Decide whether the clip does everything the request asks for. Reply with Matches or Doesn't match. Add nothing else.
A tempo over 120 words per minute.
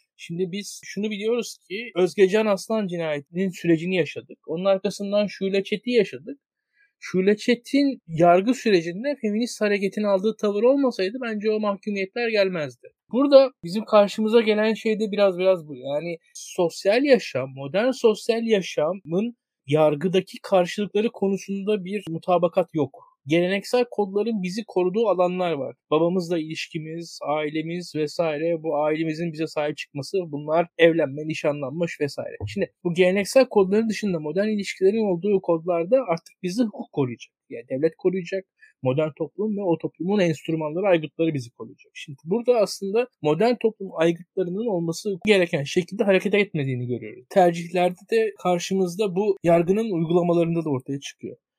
Matches